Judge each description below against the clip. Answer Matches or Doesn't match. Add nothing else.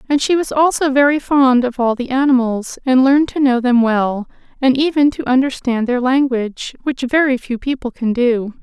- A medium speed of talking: Matches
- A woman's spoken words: Matches